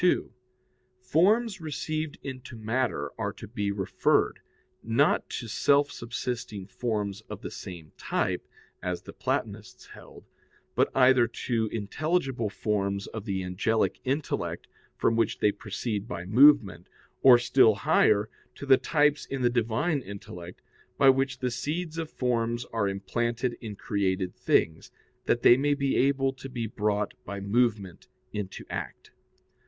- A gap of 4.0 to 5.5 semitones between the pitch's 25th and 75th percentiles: Yes, average, 4.9 semitones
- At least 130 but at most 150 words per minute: Yes, average, 140 wpm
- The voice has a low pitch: Yes, low, 115 Hz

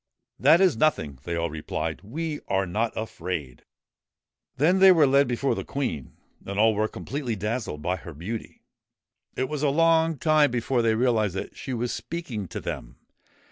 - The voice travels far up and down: Yes, wide, 7.6 semitones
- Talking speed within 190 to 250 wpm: Yes, average, 195 wpm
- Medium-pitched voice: No, low, 120 Hz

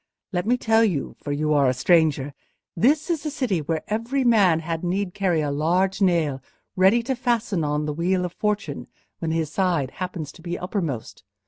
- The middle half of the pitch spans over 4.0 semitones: Yes, wide, 5.4 semitones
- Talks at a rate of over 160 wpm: Yes, average, 185 wpm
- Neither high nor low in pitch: Yes, medium, 175 Hz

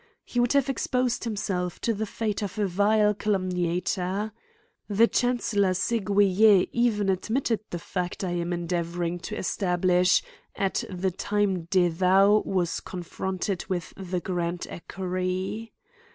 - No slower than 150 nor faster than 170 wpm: No, slow, 135 wpm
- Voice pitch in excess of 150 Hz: Yes, high, 190 Hz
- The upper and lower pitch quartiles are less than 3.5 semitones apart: Yes, average, 2.8 semitones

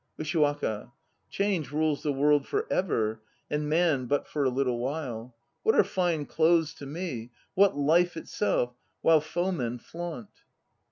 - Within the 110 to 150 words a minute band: Yes, average, 145 wpm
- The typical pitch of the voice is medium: Yes, medium, 150 Hz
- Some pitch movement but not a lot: Yes, average, 4.7 semitones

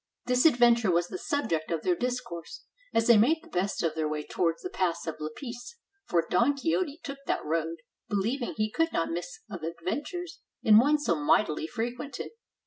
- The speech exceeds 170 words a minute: Yes, average, 190 wpm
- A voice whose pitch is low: No, high, 215 Hz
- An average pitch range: No, wide, 7.4 semitones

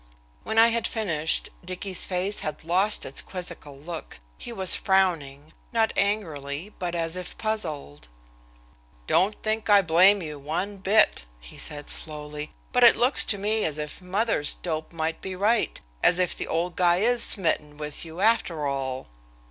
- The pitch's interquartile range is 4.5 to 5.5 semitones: Yes, average, 5.2 semitones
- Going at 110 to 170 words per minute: Yes, average, 165 wpm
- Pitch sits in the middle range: Yes, medium, 180 Hz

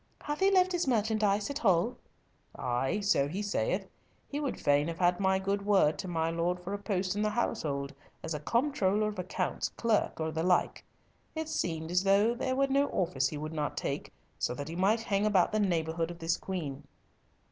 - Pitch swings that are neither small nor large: Yes, average, 4.7 semitones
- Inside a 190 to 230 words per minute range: Yes, average, 200 wpm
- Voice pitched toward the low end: No, high, 190 Hz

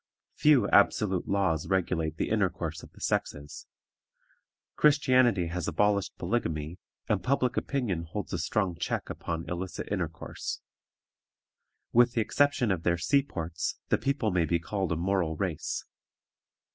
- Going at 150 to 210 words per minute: No, slow, 135 wpm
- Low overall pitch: Yes, very low, 95 Hz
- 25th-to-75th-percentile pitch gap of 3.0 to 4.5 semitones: No, wide, 5.5 semitones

